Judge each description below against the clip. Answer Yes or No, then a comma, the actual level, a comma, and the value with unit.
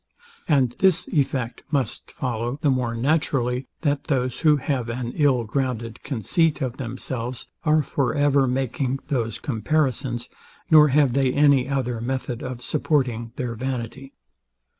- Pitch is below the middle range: Yes, low, 130 Hz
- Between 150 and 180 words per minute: No, average, 140 wpm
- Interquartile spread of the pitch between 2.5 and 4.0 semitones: Yes, average, 2.8 semitones